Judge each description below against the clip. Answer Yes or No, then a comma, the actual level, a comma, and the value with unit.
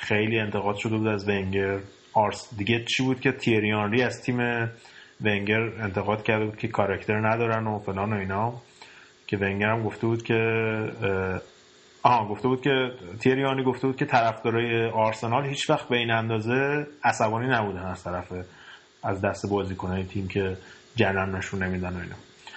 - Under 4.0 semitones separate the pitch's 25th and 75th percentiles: Yes, average, 2.9 semitones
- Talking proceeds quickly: Yes, fast, 160 wpm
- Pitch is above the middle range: No, low, 110 Hz